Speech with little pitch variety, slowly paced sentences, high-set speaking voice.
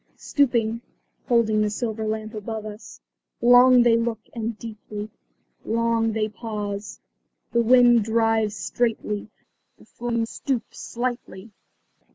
Yes: narrow, 1.6 semitones; slow, 115 wpm; high, 225 Hz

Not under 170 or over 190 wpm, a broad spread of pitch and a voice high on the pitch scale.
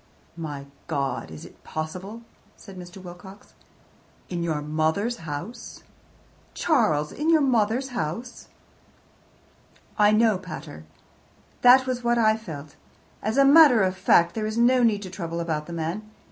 No: average, 145 wpm; wide, 6.6 semitones; high, 195 Hz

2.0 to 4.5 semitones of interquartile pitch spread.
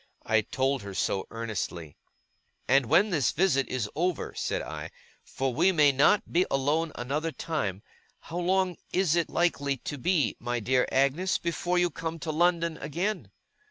No: average, 5.1 semitones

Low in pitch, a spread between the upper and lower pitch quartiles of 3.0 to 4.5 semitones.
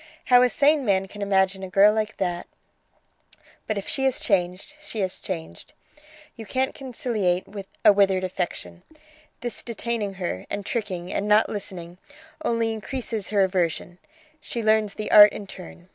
No: high, 205 Hz; average, 3.5 semitones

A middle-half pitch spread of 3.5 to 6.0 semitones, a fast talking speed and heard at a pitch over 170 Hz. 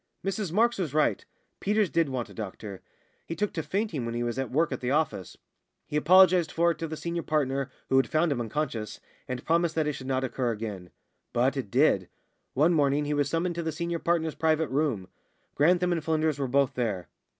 No: average, 4.5 semitones; fast, 215 wpm; medium, 155 Hz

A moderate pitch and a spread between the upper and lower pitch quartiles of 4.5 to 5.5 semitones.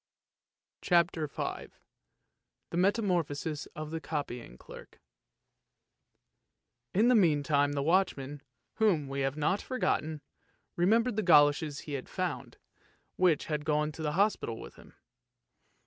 No: medium, 155 Hz; average, 4.1 semitones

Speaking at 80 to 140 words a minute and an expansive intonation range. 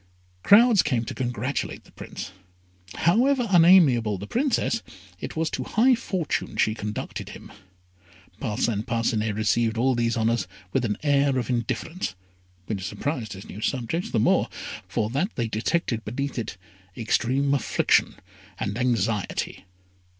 Yes: slow, 135 wpm; wide, 6.3 semitones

